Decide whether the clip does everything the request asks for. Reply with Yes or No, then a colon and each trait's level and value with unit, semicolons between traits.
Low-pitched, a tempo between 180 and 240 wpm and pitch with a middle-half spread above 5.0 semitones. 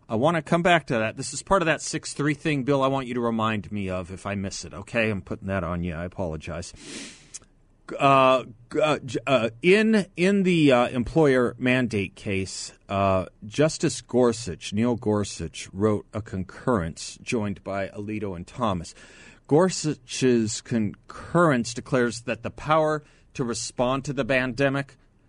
No: low, 120 Hz; average, 160 wpm; wide, 5.6 semitones